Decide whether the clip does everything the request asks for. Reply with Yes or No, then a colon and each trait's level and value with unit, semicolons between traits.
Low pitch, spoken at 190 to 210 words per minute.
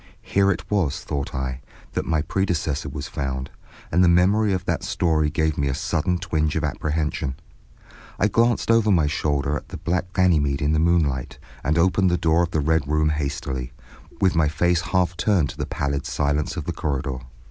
Yes: very low, 80 Hz; average, 195 wpm